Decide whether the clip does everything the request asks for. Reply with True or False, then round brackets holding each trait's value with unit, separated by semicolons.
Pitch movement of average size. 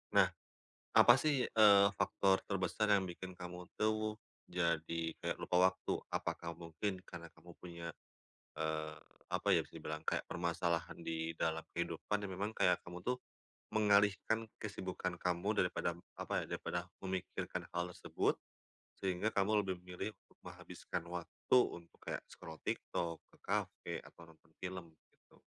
True (3.1 semitones)